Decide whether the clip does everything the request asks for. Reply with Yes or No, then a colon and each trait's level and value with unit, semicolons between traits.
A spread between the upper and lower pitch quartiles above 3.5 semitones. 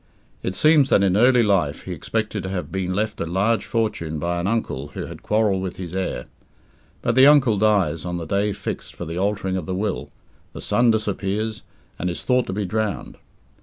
No: average, 3.2 semitones